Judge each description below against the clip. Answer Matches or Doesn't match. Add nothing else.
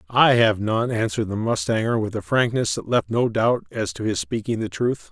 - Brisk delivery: Matches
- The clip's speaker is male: Matches